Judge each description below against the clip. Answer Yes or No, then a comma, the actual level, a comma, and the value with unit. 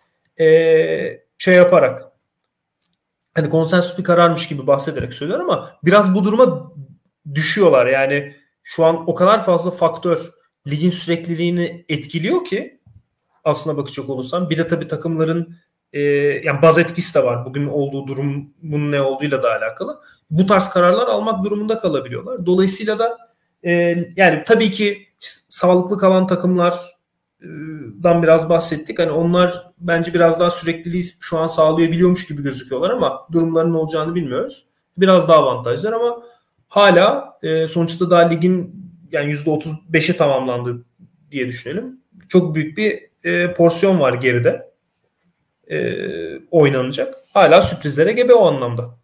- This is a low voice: No, medium, 170 Hz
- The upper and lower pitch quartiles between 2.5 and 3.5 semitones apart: Yes, average, 2.9 semitones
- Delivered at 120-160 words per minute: Yes, average, 135 wpm